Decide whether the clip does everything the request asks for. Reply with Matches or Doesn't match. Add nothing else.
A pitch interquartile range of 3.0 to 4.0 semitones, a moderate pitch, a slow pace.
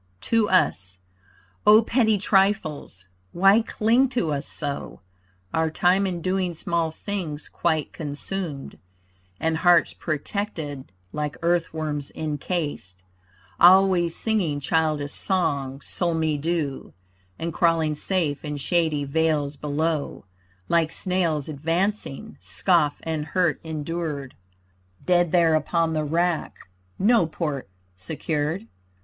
Matches